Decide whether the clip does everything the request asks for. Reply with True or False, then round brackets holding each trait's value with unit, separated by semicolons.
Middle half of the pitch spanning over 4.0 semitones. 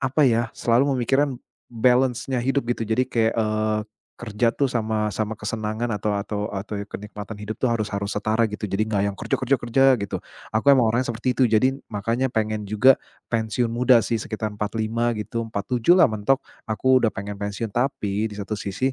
False (2.8 semitones)